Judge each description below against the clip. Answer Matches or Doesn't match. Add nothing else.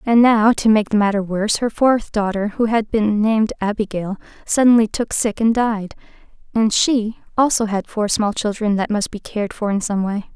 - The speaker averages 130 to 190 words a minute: Doesn't match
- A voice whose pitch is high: Matches